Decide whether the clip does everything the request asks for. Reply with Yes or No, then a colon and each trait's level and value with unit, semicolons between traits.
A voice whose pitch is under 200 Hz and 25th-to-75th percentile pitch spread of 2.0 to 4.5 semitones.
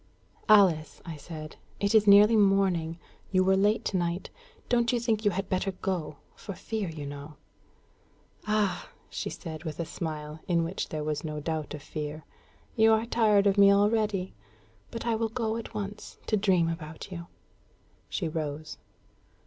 No: medium, 185 Hz; average, 4.9 semitones